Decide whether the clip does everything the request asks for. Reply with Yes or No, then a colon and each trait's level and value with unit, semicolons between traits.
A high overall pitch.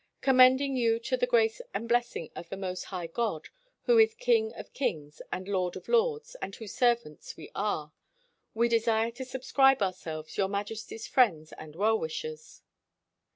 Yes: high, 225 Hz